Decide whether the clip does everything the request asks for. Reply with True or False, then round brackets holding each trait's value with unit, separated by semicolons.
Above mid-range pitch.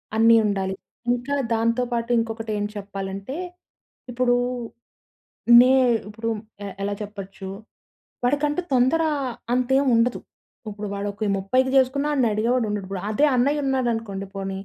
True (230 Hz)